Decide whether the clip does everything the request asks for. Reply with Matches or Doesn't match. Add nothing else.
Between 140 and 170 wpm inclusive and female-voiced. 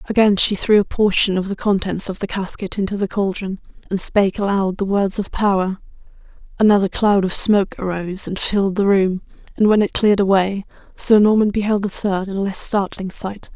Doesn't match